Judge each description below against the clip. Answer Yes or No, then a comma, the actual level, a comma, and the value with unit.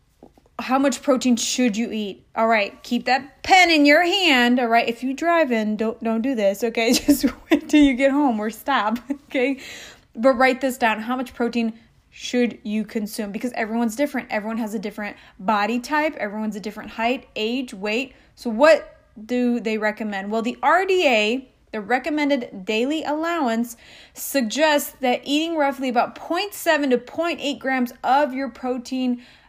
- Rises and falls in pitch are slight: No, average, 3.8 semitones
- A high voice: Yes, very high, 250 Hz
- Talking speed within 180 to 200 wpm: No, average, 170 wpm